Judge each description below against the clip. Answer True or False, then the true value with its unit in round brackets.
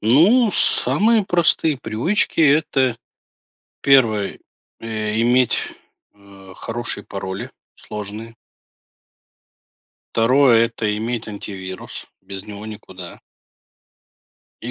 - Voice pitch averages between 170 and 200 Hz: False (115 Hz)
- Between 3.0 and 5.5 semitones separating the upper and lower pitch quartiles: True (4.5 semitones)